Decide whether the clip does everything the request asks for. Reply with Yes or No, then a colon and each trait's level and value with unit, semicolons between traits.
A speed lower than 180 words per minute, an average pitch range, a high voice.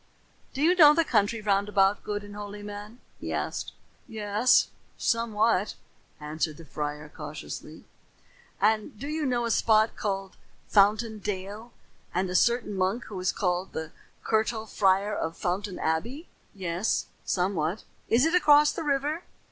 Yes: average, 150 wpm; average, 3.7 semitones; high, 205 Hz